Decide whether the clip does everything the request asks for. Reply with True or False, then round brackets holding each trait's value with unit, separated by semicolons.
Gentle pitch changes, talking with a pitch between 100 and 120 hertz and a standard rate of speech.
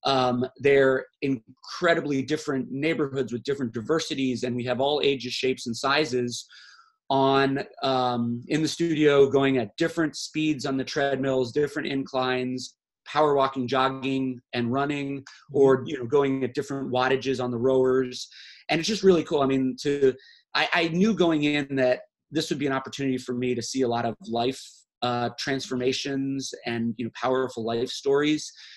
False (2.2 semitones; 135 Hz; 165 wpm)